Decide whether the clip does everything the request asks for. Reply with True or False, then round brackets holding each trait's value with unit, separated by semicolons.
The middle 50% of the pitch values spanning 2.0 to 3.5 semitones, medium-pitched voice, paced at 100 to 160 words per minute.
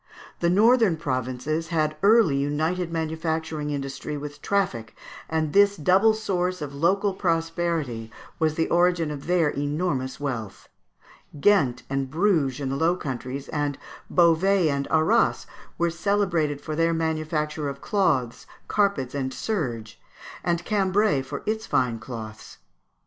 False (4.5 semitones; 160 Hz; 135 wpm)